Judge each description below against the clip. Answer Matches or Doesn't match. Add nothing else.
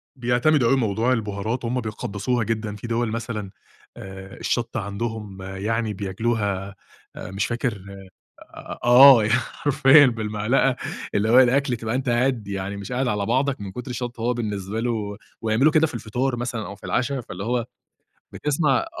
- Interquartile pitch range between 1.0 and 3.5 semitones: Matches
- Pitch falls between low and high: Doesn't match